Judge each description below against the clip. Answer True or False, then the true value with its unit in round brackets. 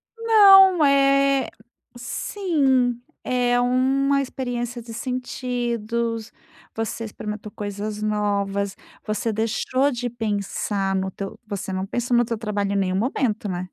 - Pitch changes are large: False (3.7 semitones)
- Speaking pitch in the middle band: False (235 Hz)